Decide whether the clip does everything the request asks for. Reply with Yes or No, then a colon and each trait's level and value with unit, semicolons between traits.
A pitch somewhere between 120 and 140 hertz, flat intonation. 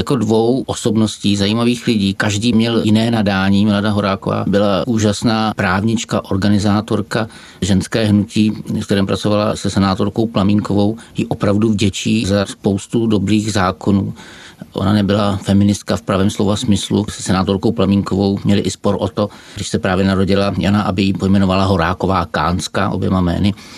No: low, 100 Hz; narrow, 1.8 semitones